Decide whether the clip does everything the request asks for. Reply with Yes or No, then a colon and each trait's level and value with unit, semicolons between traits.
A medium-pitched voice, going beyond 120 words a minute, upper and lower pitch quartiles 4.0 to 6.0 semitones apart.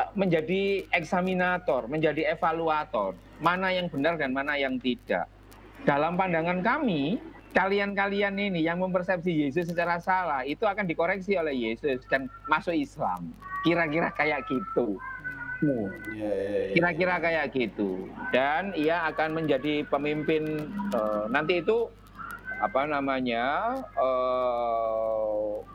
No: medium, 165 Hz; average, 105 wpm; average, 5.2 semitones